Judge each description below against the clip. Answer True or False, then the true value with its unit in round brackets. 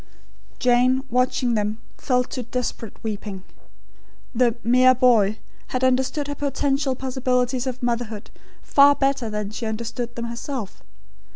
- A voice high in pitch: True (250 Hz)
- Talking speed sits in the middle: False (125 wpm)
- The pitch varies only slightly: True (2.2 semitones)